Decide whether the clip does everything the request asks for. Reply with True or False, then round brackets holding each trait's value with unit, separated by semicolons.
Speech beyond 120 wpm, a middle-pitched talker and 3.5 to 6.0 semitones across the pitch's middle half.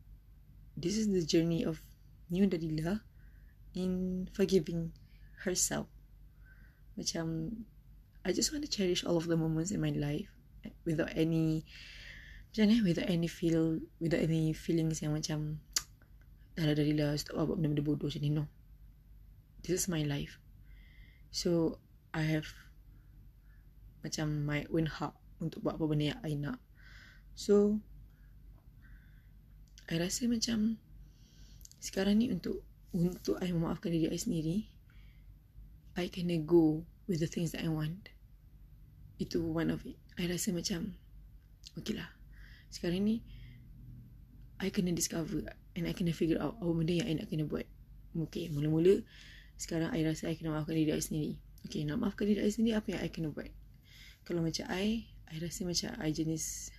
False (140 wpm; 165 Hz; 3.1 semitones)